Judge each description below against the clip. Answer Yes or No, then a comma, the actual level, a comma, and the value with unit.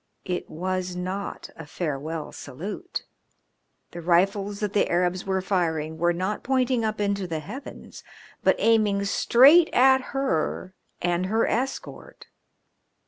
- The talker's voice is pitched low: No, high, 190 Hz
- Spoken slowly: Yes, slow, 130 wpm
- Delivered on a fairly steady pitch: No, average, 3.9 semitones